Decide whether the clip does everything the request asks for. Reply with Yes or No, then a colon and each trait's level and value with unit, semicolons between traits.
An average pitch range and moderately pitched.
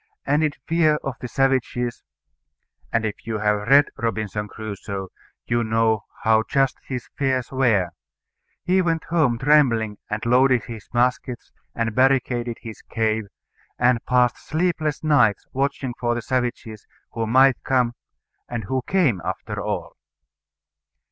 No: average, 3.3 semitones; low, 120 Hz